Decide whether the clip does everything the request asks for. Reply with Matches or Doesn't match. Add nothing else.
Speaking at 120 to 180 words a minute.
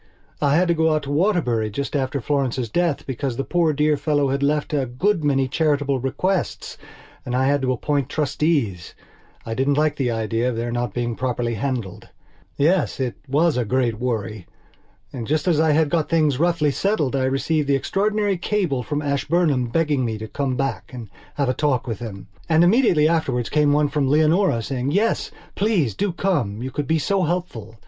Doesn't match